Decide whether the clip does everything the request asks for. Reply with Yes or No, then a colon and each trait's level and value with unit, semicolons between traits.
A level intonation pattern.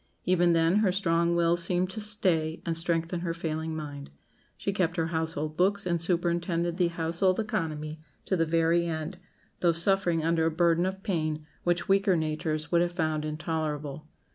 Yes: narrow, 1.9 semitones